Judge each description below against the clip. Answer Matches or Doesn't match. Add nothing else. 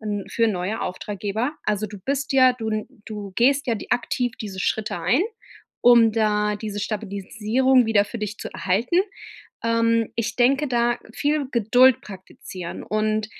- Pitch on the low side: Doesn't match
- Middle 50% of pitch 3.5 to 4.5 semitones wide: Doesn't match